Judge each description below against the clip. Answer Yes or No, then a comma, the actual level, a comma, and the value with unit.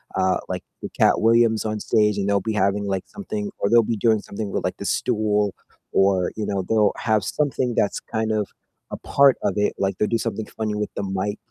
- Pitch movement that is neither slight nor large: No, narrow, 1.9 semitones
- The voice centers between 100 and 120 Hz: Yes, low, 105 Hz